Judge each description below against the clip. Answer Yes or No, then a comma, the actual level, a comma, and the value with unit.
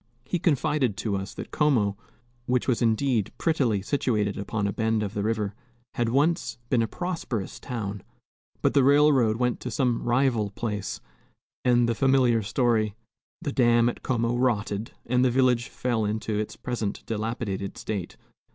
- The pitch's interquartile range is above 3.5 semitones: No, average, 3.2 semitones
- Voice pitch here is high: No, low, 115 Hz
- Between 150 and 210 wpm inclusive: Yes, average, 160 wpm